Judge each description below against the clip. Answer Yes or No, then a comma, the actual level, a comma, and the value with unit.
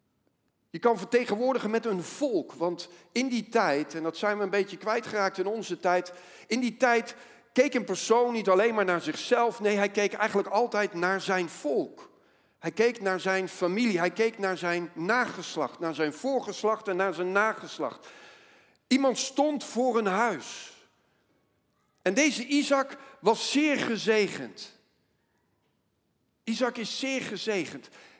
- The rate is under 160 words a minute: Yes, average, 150 wpm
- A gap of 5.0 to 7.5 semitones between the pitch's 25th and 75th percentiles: No, average, 4.4 semitones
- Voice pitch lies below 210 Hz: No, high, 215 Hz